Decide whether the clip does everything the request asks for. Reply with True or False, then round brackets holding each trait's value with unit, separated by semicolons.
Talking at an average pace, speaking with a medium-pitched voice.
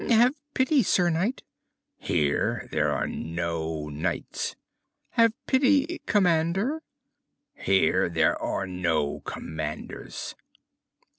False (90 wpm; 160 Hz)